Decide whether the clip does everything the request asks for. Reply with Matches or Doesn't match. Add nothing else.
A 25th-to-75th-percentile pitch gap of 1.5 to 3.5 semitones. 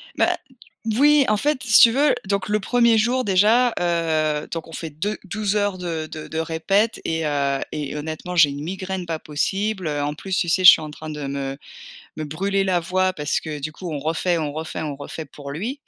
Doesn't match